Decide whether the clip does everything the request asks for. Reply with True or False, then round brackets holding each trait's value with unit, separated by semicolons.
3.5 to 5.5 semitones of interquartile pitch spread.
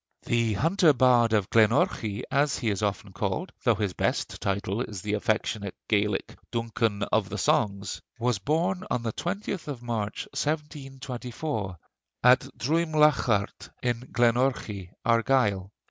True (4.7 semitones)